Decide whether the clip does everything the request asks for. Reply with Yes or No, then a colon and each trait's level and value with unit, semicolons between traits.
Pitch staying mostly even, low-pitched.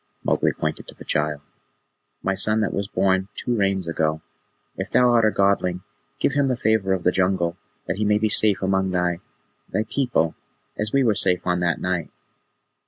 No: average, 3.4 semitones; very low, 95 Hz